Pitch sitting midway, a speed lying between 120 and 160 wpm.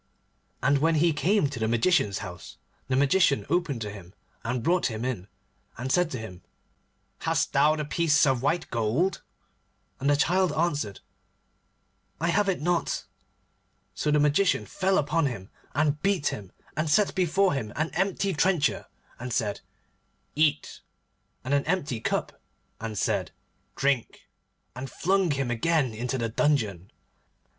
Yes: medium, 145 Hz; average, 150 wpm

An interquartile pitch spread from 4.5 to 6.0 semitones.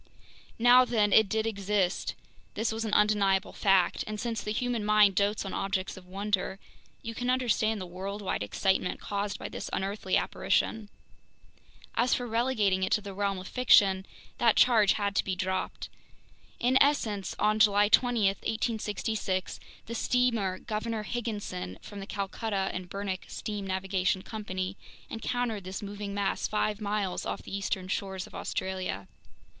No: narrow, 2.5 semitones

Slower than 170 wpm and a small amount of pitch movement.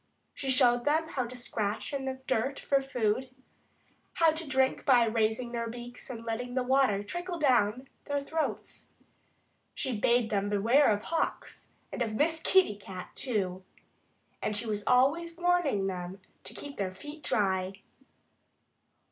No: average, 155 wpm; average, 4.9 semitones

